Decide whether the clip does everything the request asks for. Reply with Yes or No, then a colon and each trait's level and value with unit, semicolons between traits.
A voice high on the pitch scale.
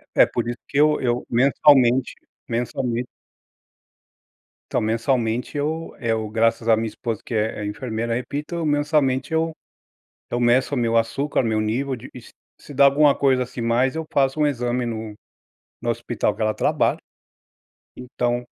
No: low, 125 Hz